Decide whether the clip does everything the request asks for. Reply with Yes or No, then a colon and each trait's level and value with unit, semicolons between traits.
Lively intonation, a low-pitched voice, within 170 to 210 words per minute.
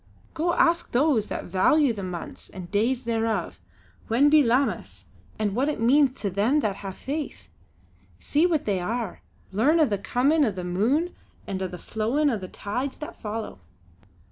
No: wide, 6.4 semitones; high, 230 Hz; average, 175 wpm